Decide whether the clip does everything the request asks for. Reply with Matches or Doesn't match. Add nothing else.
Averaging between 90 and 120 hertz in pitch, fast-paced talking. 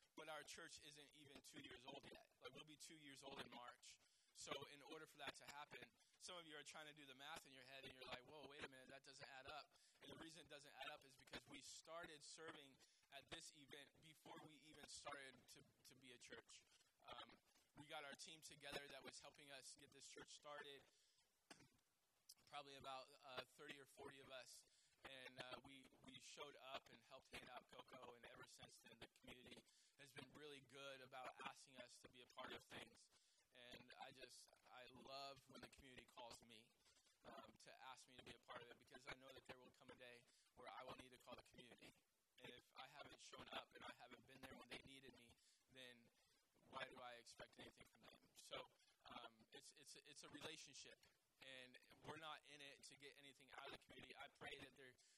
Doesn't match